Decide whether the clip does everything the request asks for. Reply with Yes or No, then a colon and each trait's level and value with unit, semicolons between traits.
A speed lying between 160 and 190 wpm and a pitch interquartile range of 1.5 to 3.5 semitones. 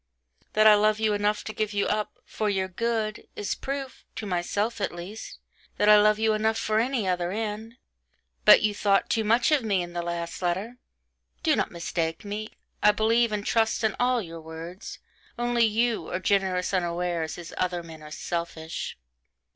No: average, 185 wpm; average, 3.9 semitones